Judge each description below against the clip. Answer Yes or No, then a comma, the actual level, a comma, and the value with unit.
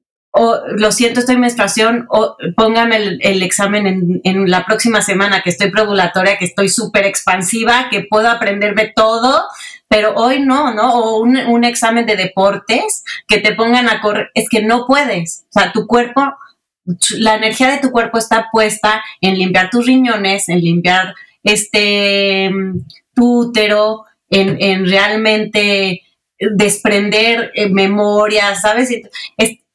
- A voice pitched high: Yes, high, 215 Hz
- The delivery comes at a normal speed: Yes, average, 145 wpm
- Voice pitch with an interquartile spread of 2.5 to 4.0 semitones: Yes, average, 2.8 semitones